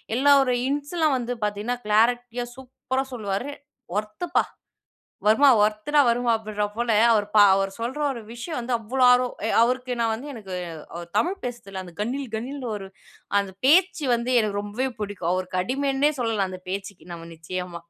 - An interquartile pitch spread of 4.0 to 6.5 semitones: Yes, average, 4.4 semitones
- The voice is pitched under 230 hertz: No, high, 235 Hz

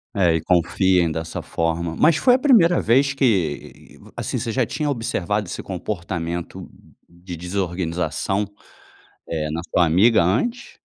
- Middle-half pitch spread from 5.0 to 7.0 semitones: Yes, wide, 5.6 semitones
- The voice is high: No, very low, 90 Hz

